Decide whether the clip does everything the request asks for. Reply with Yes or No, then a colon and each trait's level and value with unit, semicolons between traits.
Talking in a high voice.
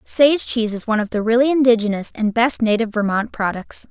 Yes: high, 225 Hz